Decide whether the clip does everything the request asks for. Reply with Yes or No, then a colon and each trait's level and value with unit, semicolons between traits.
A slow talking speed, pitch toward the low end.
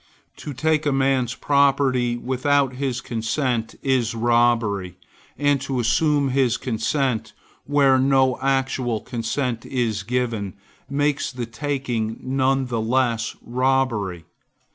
Yes: slow, 115 wpm; low, 130 Hz